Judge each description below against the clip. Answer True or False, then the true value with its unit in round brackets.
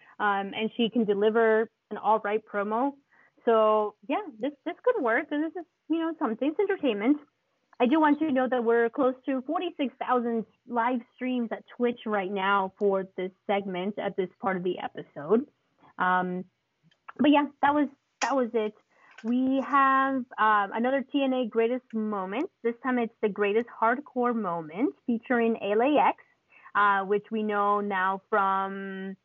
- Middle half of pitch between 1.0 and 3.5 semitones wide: False (4.7 semitones)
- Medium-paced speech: True (165 wpm)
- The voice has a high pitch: True (230 Hz)